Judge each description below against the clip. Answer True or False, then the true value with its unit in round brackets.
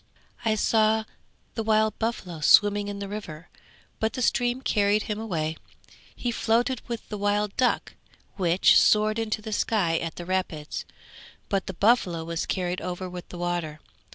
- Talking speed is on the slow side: False (160 wpm)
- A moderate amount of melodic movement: True (3.9 semitones)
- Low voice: False (205 Hz)